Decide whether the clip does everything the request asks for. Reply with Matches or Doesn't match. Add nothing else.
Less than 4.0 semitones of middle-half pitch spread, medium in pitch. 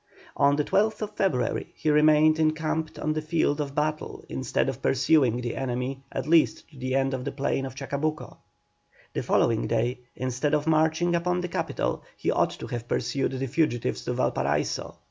Matches